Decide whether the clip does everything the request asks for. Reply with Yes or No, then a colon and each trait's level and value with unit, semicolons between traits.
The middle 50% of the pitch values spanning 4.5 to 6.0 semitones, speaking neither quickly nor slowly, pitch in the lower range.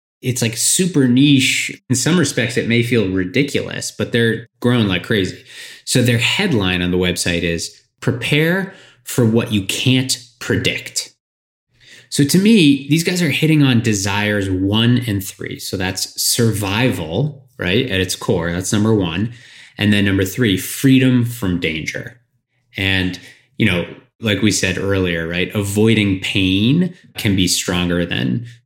Yes: average, 5.0 semitones; average, 150 wpm; low, 115 Hz